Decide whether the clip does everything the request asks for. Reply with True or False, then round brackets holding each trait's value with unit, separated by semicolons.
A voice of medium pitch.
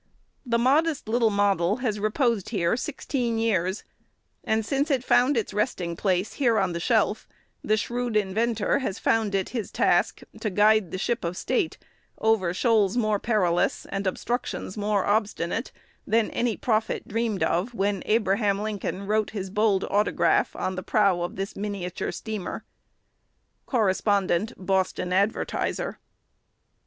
False (210 Hz)